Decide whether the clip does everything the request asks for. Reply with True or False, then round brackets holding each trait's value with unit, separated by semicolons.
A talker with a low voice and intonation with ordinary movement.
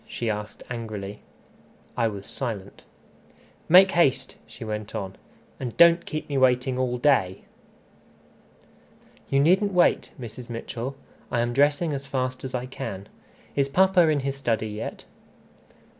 True (130 Hz; 4.1 semitones)